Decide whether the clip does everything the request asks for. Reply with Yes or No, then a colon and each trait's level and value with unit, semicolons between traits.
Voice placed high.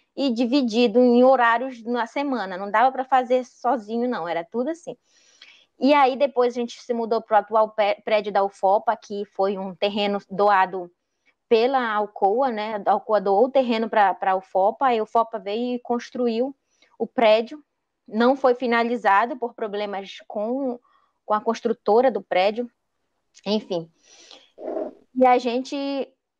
Yes: high, 230 Hz